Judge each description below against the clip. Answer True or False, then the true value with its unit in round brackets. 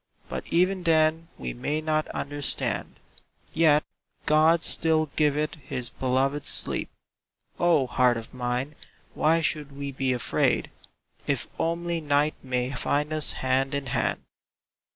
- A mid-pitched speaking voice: True (145 Hz)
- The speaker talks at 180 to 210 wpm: False (135 wpm)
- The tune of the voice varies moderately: True (3.1 semitones)